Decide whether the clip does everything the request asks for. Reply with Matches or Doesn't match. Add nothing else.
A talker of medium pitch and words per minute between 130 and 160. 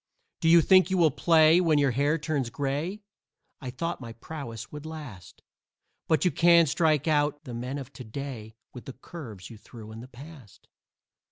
Doesn't match